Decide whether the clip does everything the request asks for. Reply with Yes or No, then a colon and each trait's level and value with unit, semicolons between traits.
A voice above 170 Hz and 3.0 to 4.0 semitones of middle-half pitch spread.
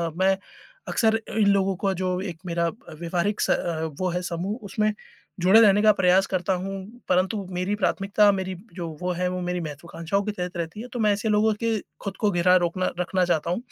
No: high, 190 Hz; narrow, 2.5 semitones